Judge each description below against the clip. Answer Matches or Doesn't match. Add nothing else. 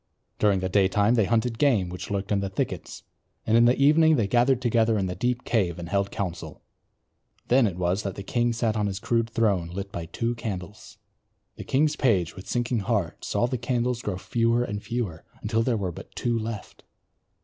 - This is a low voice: Matches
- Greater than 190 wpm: Matches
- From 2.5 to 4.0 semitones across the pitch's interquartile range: Matches